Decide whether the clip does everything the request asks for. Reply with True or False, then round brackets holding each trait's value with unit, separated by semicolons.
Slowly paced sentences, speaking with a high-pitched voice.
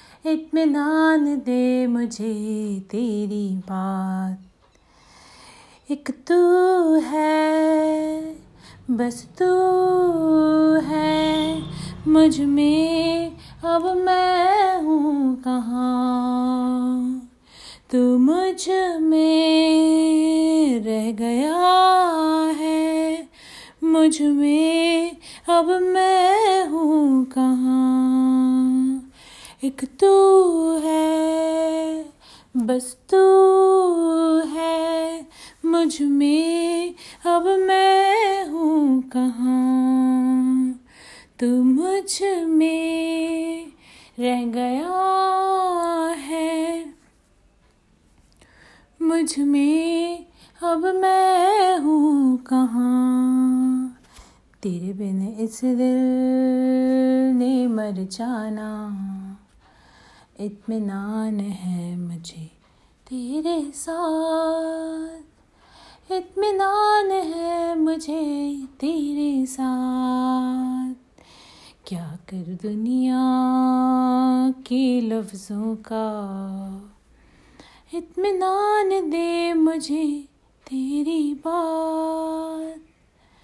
True (60 wpm; 305 Hz)